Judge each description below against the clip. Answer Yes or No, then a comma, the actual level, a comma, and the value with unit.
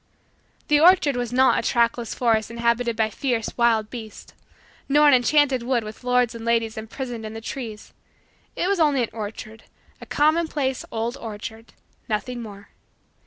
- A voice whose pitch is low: No, high, 235 Hz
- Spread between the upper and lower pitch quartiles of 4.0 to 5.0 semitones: No, average, 2.9 semitones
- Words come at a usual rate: Yes, average, 160 wpm